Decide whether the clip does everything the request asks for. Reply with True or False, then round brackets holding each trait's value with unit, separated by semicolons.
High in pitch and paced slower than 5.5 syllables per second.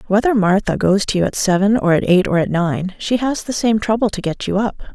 False (200 Hz; 5.6 syllables/s)